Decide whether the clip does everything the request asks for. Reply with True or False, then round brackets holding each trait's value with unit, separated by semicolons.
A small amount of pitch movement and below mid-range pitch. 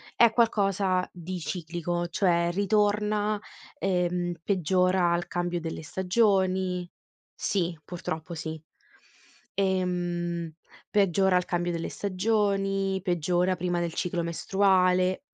False (2.1 semitones; 180 Hz)